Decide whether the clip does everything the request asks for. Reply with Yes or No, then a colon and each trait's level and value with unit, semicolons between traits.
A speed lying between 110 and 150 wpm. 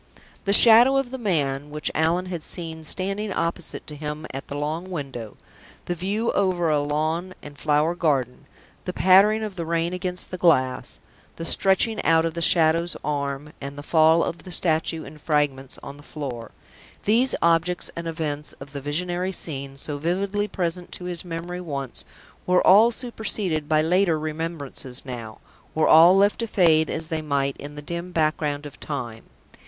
No: average, 175 wpm